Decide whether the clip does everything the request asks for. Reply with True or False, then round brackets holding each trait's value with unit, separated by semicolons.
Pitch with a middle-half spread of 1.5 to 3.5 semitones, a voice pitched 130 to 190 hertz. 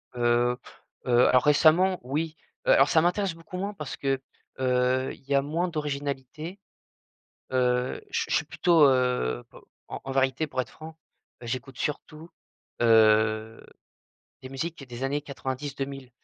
False (3.9 semitones; 135 Hz)